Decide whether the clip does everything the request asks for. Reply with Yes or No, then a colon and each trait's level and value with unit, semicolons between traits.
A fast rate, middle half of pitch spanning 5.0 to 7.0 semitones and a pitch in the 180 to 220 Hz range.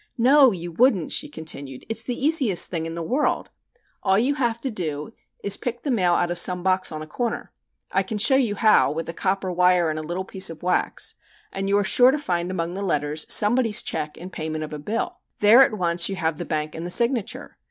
Yes: fast, 235 wpm; wide, 5.6 semitones; medium, 185 Hz